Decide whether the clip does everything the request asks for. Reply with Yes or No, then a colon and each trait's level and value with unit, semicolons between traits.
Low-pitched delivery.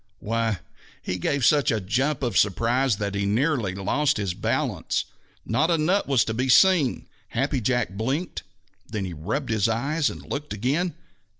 Yes: low, 120 Hz